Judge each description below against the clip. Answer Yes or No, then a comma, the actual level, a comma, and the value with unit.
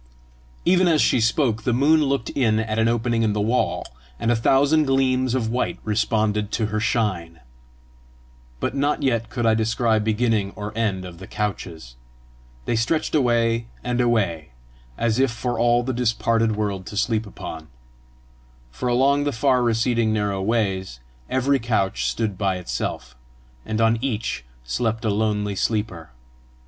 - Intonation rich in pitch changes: No, average, 2.8 semitones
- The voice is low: Yes, low, 115 Hz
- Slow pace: No, average, 155 wpm